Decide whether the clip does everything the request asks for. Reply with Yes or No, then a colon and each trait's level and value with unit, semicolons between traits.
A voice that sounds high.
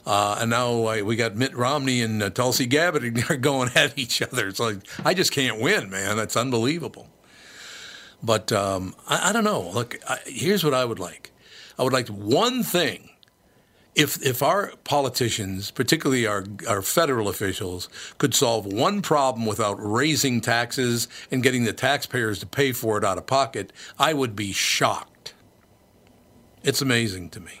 No: low, 120 Hz